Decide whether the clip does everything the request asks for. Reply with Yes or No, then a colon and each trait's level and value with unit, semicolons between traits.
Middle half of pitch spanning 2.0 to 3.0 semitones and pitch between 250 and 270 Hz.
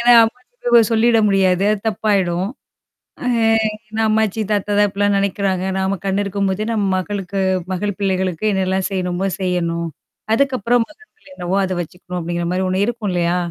No: average, 2.7 semitones; high, 195 Hz